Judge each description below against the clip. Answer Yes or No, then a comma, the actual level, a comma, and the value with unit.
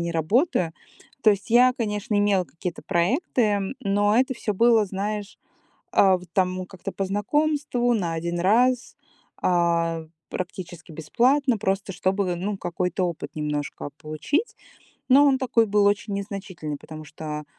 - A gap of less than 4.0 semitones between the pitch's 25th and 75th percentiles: No, average, 4.7 semitones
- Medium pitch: No, high, 195 Hz